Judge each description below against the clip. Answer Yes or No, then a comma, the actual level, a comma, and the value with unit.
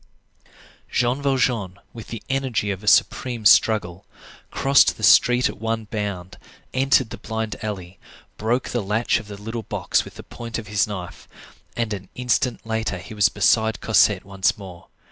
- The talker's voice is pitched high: No, low, 110 Hz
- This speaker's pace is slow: No, average, 165 wpm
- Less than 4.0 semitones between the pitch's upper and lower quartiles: Yes, average, 3.0 semitones